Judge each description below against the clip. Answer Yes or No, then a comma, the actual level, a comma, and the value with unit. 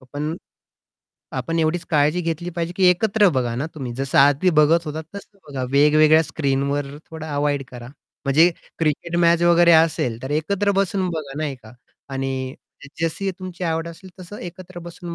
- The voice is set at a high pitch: No, medium, 160 Hz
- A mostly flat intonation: No, average, 3.5 semitones